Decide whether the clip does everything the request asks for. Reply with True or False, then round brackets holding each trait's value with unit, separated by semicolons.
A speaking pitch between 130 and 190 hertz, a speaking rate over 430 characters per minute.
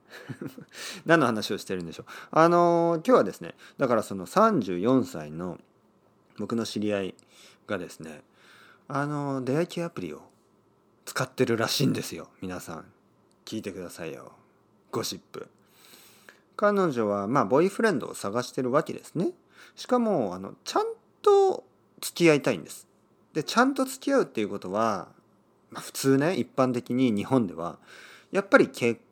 False (135 Hz; 305 characters per minute)